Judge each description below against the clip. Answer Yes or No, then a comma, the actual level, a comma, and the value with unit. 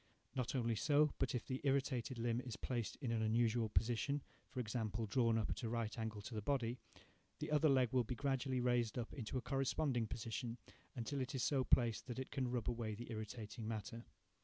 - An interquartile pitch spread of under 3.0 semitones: Yes, narrow, 2.5 semitones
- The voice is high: No, low, 120 Hz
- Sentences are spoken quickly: Yes, fast, 210 wpm